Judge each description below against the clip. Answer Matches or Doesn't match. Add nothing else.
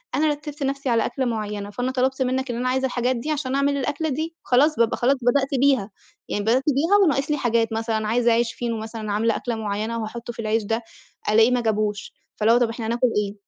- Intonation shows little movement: Doesn't match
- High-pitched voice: Matches